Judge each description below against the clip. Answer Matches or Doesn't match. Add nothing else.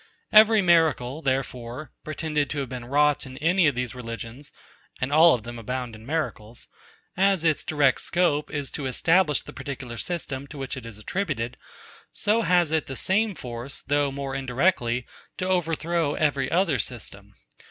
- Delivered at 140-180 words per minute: Matches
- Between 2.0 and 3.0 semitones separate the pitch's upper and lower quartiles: Doesn't match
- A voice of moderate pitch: Matches